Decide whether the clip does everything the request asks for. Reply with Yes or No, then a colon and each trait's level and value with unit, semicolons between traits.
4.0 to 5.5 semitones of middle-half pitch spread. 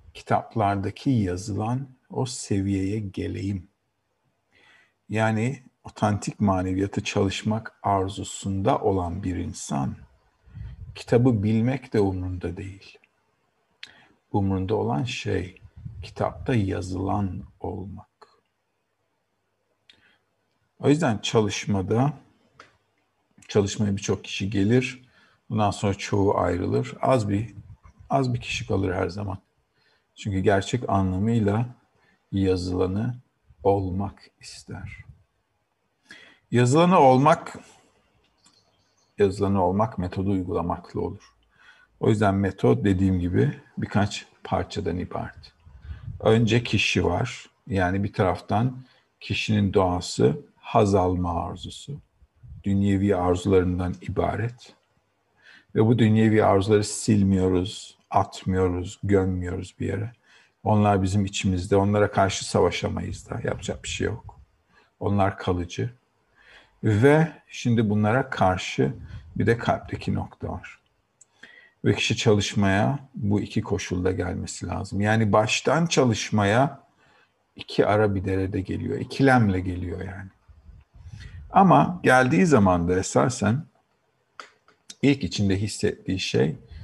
No: average, 3.0 semitones